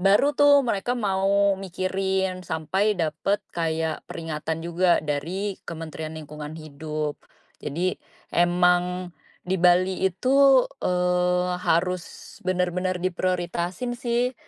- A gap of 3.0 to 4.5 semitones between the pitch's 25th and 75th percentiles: No, narrow, 2.6 semitones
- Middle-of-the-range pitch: Yes, medium, 180 Hz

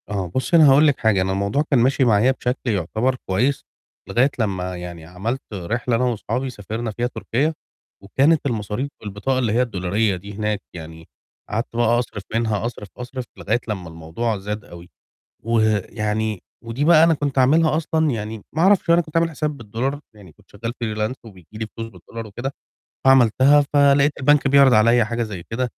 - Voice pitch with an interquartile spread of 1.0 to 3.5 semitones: No, average, 4.4 semitones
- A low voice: Yes, low, 115 Hz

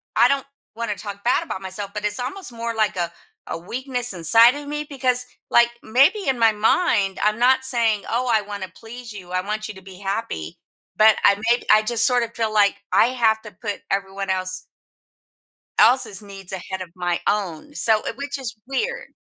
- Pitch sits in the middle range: No, high, 220 Hz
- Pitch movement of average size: Yes, average, 3.9 semitones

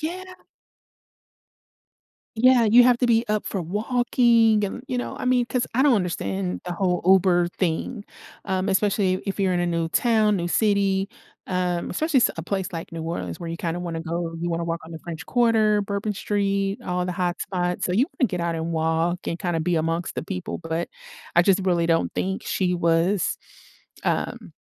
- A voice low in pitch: No, medium, 185 Hz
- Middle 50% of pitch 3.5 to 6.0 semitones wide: Yes, average, 3.9 semitones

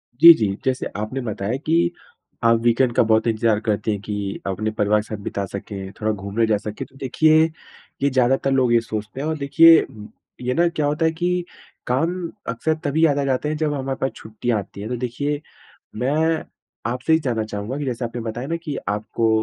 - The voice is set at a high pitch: No, low, 125 Hz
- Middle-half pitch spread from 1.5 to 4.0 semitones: No, average, 5.3 semitones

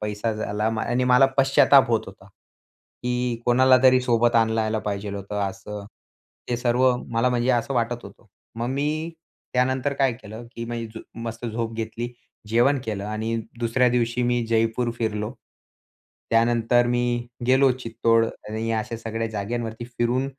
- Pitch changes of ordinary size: No, narrow, 1.9 semitones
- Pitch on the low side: Yes, low, 115 Hz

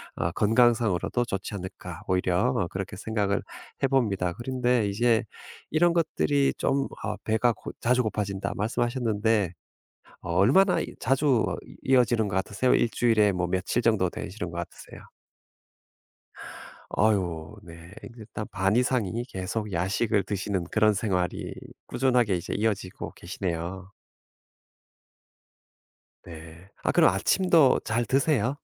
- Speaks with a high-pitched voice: No, low, 105 Hz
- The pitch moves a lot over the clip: No, average, 4.5 semitones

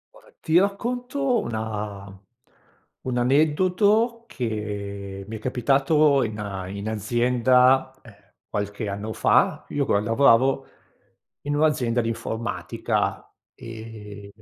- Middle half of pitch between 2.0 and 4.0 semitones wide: No, wide, 5.7 semitones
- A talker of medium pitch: No, low, 115 Hz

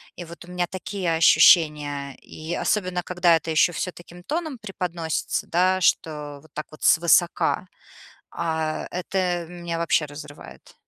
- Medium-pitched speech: Yes, medium, 170 Hz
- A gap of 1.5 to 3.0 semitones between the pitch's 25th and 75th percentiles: Yes, narrow, 2.4 semitones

